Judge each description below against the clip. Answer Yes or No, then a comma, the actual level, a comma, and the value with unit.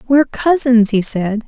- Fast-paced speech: No, average, 160 wpm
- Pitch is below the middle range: No, high, 240 Hz